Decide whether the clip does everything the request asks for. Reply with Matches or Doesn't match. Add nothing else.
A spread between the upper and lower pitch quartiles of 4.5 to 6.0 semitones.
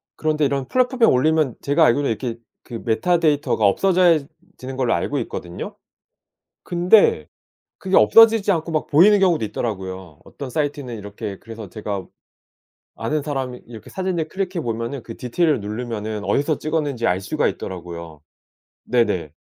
Doesn't match